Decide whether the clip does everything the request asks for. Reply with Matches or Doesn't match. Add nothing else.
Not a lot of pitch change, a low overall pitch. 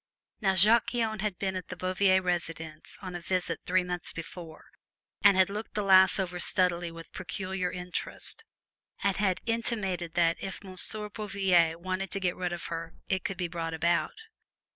Doesn't match